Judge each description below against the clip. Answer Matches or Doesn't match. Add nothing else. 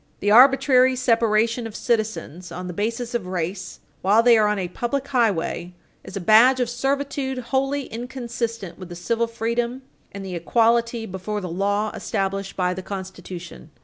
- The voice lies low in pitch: Doesn't match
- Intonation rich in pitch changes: Doesn't match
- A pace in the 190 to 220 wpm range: Doesn't match